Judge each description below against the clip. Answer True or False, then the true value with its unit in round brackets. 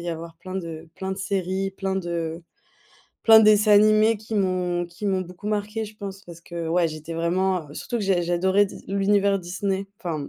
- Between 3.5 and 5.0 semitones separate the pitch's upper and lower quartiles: False (2.8 semitones)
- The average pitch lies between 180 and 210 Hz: True (190 Hz)